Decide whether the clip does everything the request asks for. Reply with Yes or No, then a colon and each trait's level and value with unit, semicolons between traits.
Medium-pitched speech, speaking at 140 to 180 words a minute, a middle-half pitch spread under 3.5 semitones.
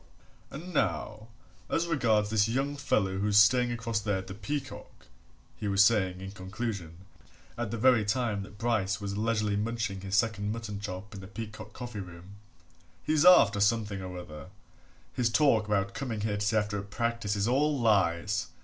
No: low, 105 Hz; average, 175 wpm; average, 2.8 semitones